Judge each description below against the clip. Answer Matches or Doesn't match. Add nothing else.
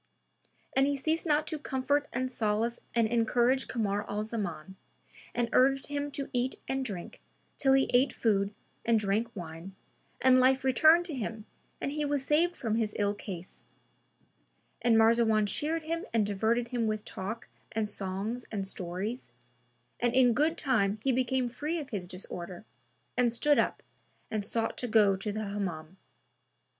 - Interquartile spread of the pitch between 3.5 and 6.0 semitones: Matches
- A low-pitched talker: Doesn't match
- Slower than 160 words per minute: Doesn't match